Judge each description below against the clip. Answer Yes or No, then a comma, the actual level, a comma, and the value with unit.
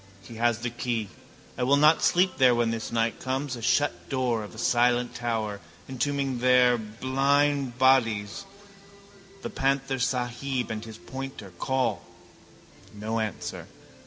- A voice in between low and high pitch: No, low, 125 Hz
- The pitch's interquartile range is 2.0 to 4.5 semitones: Yes, average, 2.8 semitones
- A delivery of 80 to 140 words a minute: Yes, slow, 135 wpm